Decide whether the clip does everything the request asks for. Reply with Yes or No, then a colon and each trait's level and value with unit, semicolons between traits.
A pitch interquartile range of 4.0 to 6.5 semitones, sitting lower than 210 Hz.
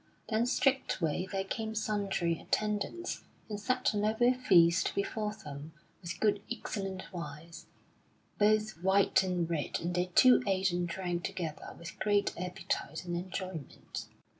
No: average, 3.6 semitones; high, 190 Hz